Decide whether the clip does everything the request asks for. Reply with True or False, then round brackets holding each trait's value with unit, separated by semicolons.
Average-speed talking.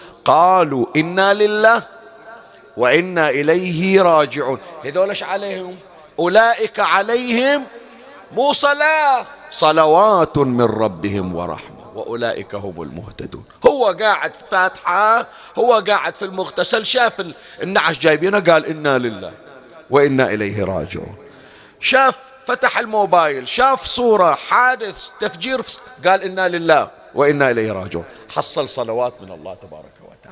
True (105 wpm)